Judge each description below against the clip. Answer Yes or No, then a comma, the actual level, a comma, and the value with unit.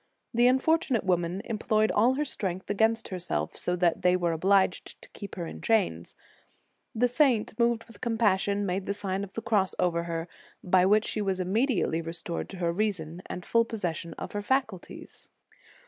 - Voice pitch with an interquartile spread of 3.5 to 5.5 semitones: Yes, average, 4.1 semitones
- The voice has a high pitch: Yes, high, 200 Hz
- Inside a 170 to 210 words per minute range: Yes, average, 180 wpm